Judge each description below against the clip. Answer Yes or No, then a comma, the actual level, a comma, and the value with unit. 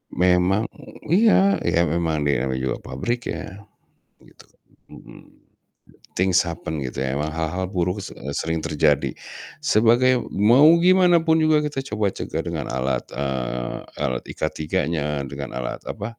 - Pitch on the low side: Yes, very low, 85 Hz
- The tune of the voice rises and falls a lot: Yes, wide, 8.4 semitones